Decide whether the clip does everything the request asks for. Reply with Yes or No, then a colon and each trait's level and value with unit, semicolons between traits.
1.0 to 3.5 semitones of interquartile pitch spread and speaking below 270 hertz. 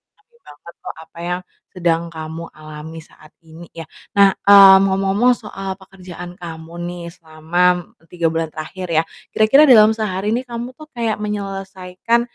No: average, 4.4 semitones; medium, 185 Hz